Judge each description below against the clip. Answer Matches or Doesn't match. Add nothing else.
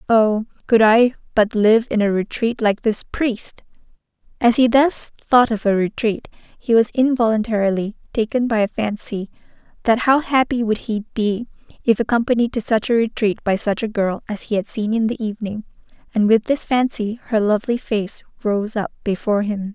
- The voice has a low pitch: Doesn't match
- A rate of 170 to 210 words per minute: Matches